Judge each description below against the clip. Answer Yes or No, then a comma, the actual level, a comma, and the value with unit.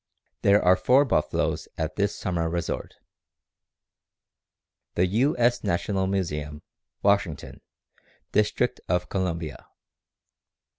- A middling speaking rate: No, slow, 100 wpm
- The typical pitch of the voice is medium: No, very low, 90 Hz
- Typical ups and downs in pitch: Yes, average, 3.5 semitones